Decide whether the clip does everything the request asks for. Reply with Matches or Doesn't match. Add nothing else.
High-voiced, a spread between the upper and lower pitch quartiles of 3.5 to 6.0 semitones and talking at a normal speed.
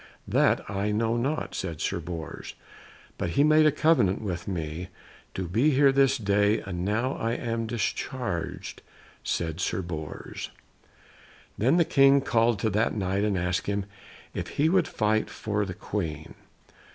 Doesn't match